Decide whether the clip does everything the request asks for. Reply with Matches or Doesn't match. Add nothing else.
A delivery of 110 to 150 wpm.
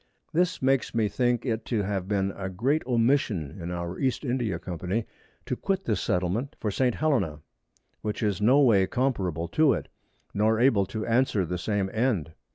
Doesn't match